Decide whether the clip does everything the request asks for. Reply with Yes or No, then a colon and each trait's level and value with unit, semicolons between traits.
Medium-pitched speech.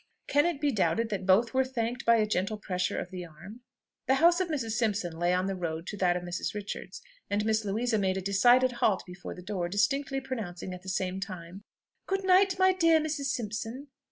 No: high, 215 Hz